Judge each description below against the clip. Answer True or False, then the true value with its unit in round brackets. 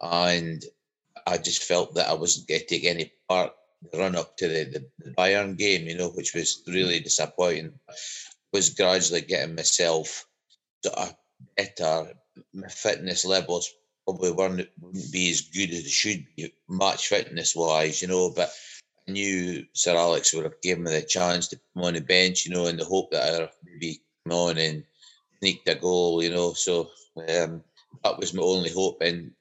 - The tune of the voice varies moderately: False (1.6 semitones)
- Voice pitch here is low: True (90 Hz)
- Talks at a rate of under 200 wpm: True (180 wpm)